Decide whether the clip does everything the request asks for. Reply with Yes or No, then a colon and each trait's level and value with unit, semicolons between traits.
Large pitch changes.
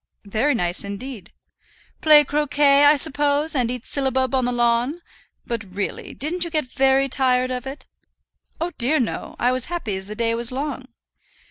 No: average, 3.6 semitones